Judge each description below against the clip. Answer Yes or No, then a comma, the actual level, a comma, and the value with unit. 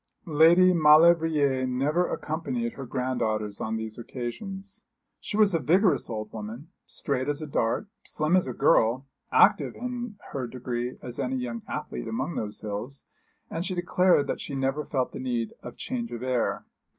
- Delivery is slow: No, average, 165 wpm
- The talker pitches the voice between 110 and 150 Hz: Yes, low, 135 Hz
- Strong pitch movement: Yes, wide, 6.1 semitones